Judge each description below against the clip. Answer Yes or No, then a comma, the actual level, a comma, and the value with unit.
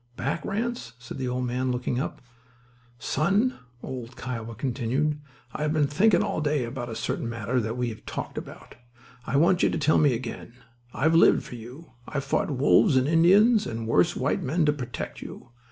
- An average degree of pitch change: Yes, average, 4.4 semitones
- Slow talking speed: No, average, 185 wpm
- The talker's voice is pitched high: No, low, 135 Hz